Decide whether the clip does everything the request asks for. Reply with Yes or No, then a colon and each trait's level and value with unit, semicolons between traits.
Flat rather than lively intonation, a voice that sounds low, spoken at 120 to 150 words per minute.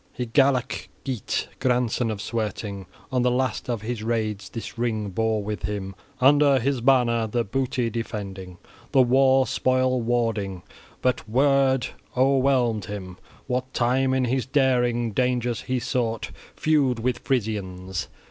No: average, 3.1 semitones; low, 120 Hz; slow, 135 wpm